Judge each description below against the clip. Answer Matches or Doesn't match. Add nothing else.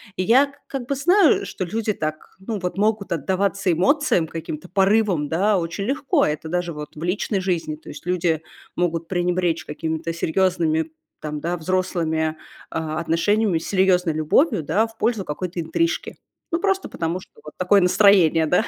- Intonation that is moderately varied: Matches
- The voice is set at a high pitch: Doesn't match